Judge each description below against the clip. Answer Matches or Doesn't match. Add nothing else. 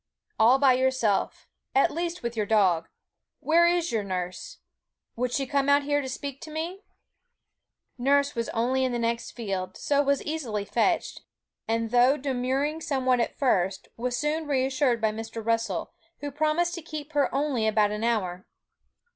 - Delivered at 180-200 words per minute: Doesn't match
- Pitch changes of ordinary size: Matches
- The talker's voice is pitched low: Doesn't match